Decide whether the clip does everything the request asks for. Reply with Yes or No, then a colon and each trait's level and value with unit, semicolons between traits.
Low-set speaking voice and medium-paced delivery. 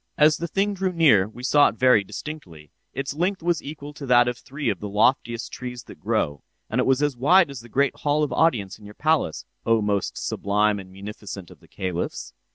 No: low, 125 Hz; fast, 220 wpm